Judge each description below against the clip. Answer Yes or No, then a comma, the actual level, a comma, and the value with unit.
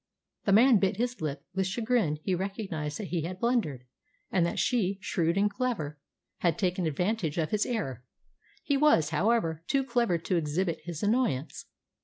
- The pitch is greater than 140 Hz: Yes, high, 190 Hz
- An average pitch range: No, wide, 5.9 semitones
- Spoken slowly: No, average, 170 wpm